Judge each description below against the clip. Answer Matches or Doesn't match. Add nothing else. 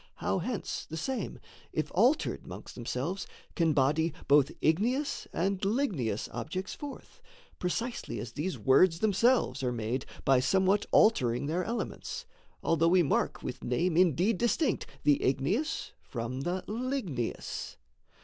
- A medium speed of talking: Doesn't match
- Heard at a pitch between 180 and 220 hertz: Doesn't match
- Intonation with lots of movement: Matches